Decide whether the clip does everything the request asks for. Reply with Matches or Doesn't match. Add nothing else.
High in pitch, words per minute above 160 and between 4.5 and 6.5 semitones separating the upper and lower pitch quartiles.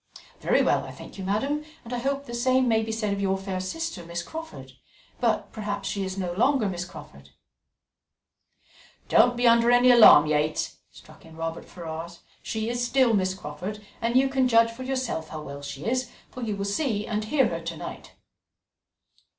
Matches